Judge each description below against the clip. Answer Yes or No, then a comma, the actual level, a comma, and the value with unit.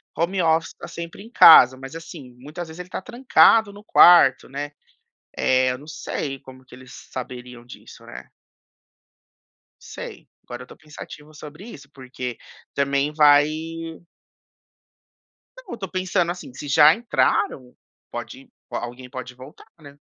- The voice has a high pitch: No, medium, 145 Hz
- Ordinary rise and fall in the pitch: Yes, average, 4.6 semitones